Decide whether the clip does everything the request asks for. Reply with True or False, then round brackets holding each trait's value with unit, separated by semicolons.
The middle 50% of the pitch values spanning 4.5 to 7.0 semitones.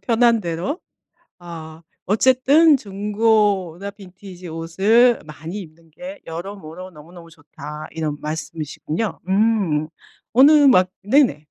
True (5.5 semitones)